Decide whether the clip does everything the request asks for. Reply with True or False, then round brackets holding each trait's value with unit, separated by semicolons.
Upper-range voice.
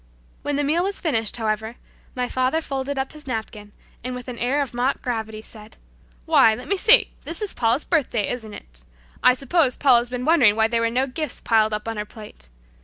True (245 Hz)